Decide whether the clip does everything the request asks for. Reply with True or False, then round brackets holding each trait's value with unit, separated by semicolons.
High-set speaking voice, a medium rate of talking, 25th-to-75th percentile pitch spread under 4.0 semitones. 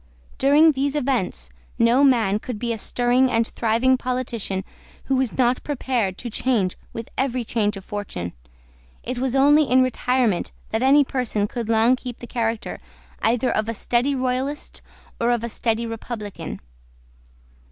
True (240 Hz; 155 wpm; 2.7 semitones)